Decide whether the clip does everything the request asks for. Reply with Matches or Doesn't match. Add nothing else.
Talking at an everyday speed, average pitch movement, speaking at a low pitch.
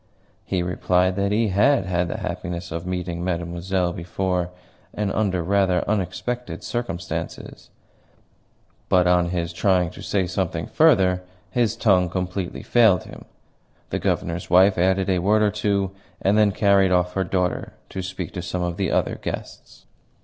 Doesn't match